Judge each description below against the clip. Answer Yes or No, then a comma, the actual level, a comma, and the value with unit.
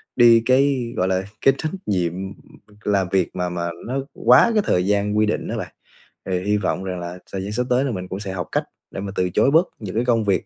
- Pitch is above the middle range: No, low, 100 Hz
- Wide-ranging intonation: No, average, 4.6 semitones